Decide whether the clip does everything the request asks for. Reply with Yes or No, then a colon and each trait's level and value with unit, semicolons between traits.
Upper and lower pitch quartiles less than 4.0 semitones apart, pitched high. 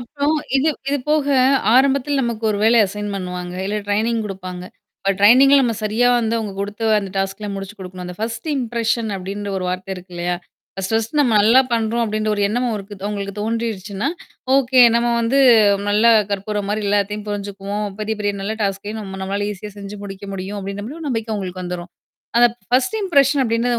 Yes: average, 3.0 semitones; high, 210 Hz